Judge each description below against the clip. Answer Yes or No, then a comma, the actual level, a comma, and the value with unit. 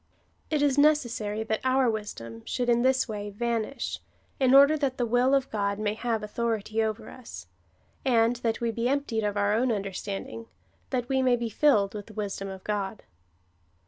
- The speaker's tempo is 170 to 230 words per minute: Yes, average, 185 wpm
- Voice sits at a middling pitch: No, high, 230 Hz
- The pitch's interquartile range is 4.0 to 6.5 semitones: No, average, 3.6 semitones